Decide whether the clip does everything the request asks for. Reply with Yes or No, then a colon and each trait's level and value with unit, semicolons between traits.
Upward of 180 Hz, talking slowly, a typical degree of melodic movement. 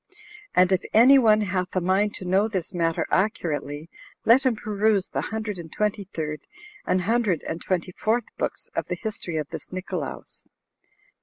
No: high, 190 Hz; average, 170 wpm; average, 3.5 semitones